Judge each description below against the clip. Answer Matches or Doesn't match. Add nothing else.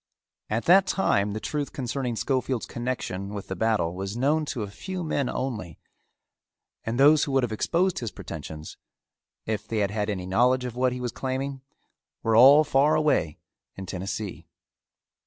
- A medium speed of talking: Matches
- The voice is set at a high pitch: Doesn't match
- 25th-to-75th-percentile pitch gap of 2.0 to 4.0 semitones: Doesn't match